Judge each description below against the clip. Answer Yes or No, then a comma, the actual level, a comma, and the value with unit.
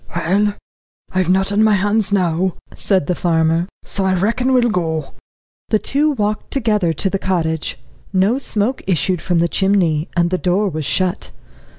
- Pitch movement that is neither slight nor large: Yes, average, 3.4 semitones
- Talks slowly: No, average, 175 wpm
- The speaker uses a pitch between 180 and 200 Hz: Yes, high, 190 Hz